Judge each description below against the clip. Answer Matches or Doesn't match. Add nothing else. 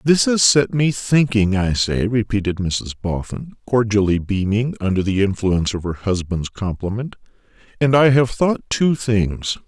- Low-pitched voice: Matches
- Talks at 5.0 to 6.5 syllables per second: Doesn't match